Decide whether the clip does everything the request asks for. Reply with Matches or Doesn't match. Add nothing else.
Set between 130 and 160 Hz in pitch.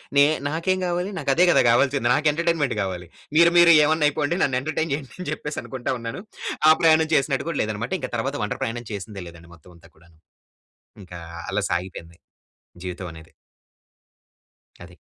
Matches